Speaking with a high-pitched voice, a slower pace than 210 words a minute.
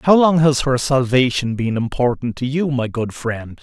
No: low, 130 Hz; average, 200 wpm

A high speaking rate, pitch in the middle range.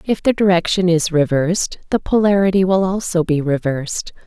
No: average, 155 wpm; medium, 180 Hz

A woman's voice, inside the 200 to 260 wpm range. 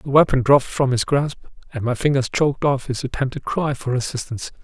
No: male; fast, 205 wpm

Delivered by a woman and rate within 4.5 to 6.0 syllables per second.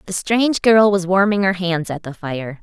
Yes: female; 4.9 syllables/s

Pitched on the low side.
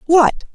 No: very high, 305 Hz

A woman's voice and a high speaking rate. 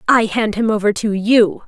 Yes: female; fast, 215 wpm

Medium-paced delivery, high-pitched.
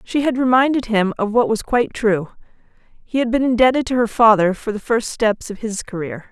No: fast, 220 wpm; high, 225 Hz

